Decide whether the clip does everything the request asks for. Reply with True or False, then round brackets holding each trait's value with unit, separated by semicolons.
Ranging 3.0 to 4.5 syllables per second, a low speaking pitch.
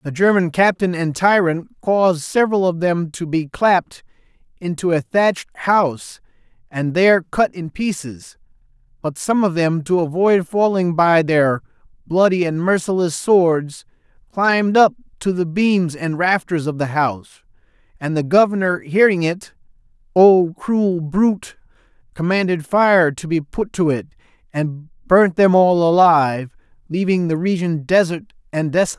False (4.4 syllables/s; 175 Hz)